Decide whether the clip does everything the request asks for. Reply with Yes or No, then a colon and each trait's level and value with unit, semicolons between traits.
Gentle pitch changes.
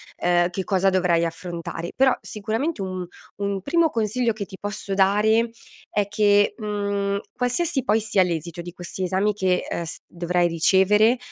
No: average, 3.1 semitones